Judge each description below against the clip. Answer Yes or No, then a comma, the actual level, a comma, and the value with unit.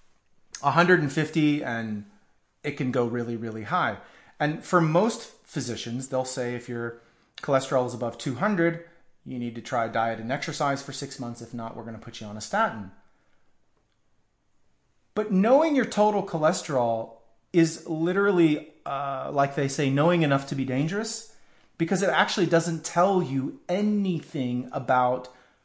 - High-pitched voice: No, medium, 140 Hz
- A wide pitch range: Yes, wide, 6.1 semitones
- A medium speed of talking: Yes, average, 150 wpm